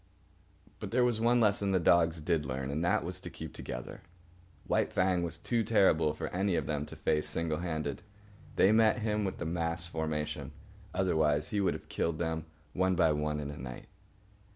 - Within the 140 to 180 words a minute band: No, average, 195 wpm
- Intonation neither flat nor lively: Yes, average, 4.0 semitones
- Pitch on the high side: No, very low, 85 Hz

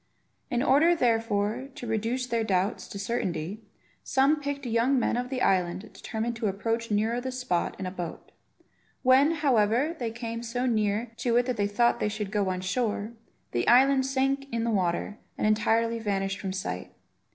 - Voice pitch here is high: Yes, high, 230 Hz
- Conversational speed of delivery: Yes, average, 180 wpm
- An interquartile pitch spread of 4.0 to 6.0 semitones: No, average, 3.6 semitones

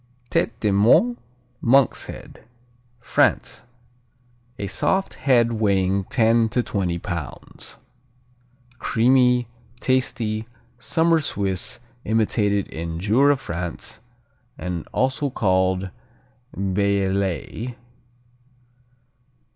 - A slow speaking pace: Yes, slow, 80 wpm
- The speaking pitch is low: Yes, low, 110 Hz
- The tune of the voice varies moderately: Yes, average, 4.6 semitones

